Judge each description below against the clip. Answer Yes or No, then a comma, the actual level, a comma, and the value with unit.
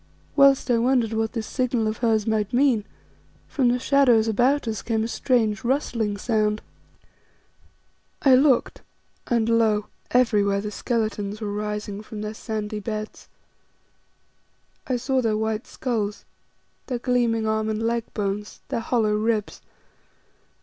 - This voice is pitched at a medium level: No, high, 225 Hz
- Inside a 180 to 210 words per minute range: No, slow, 135 wpm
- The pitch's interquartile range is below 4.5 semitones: Yes, narrow, 2.4 semitones